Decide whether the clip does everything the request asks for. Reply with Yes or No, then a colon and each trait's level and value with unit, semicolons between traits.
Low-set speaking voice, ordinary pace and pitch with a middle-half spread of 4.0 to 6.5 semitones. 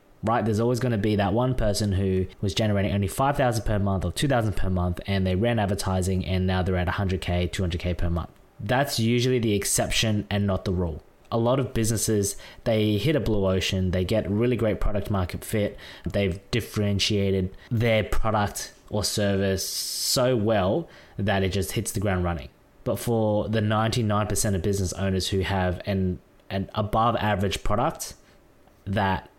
No: low, 100 Hz; average, 175 wpm; average, 2.8 semitones